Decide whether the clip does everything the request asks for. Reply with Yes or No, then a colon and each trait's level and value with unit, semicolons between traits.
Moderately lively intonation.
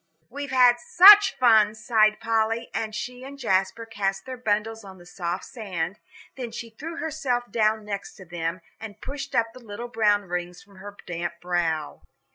Yes: average, 4.0 semitones